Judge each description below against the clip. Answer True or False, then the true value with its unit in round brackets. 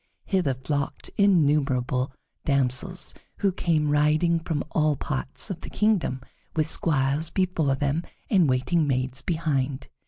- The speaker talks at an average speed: False (125 wpm)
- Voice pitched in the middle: True (150 Hz)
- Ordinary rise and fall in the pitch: True (3.9 semitones)